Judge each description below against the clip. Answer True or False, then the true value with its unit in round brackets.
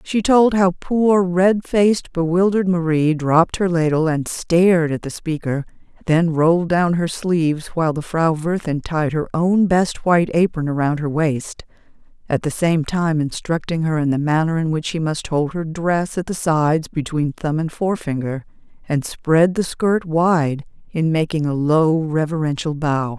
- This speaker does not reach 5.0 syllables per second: True (4.5 syllables/s)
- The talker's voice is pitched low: False (165 Hz)